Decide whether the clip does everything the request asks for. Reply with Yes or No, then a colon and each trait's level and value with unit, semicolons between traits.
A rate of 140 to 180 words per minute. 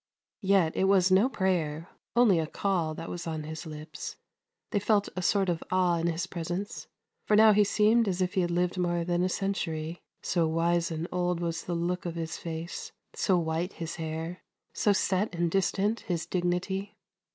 No: average, 190 wpm